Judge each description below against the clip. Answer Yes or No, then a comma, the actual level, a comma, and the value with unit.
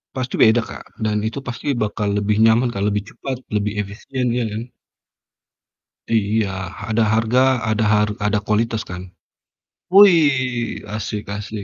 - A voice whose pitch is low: Yes, low, 110 Hz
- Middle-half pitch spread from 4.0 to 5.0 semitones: No, narrow, 2.6 semitones